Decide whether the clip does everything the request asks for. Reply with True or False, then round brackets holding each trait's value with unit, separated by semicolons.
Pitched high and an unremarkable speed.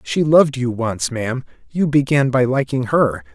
False (130 Hz; 180 wpm)